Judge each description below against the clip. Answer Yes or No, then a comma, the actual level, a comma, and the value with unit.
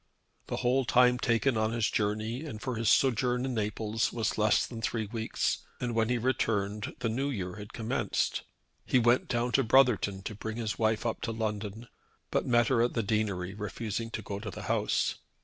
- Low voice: Yes, low, 115 Hz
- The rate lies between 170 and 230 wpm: Yes, average, 200 wpm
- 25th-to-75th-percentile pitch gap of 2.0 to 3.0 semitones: Yes, narrow, 2.4 semitones